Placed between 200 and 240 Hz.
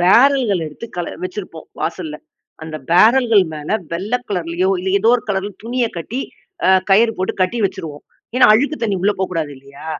No: high, 190 Hz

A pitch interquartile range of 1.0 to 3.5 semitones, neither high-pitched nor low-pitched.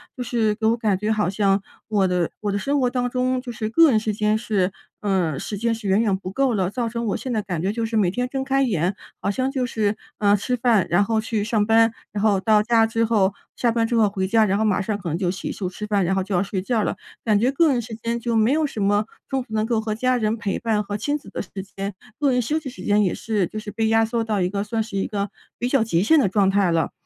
No: average, 2.8 semitones; high, 215 Hz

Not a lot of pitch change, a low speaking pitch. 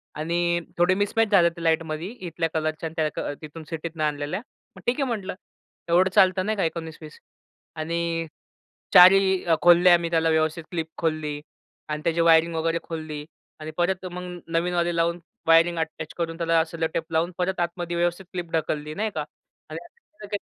No: narrow, 1.7 semitones; medium, 170 Hz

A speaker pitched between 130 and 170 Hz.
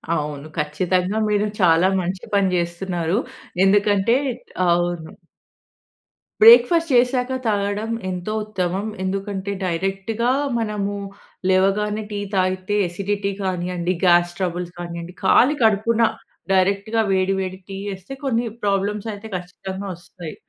No: high, 195 Hz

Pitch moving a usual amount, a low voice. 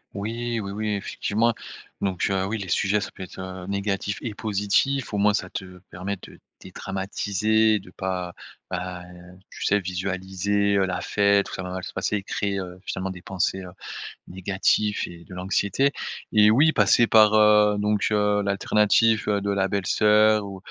No: narrow, 2.0 semitones; low, 100 Hz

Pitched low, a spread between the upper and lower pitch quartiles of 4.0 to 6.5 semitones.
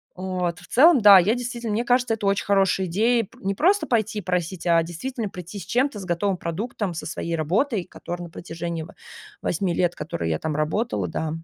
No: high, 190 Hz; average, 5.0 semitones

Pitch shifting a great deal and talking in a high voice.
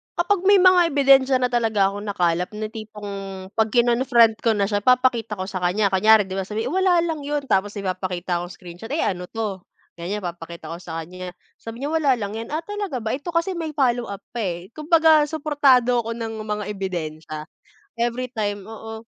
Yes: wide, 6.0 semitones; high, 220 Hz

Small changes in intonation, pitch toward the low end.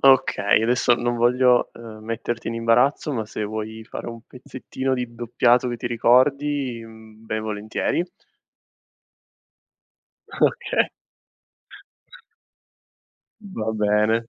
Yes: narrow, 2.2 semitones; low, 115 Hz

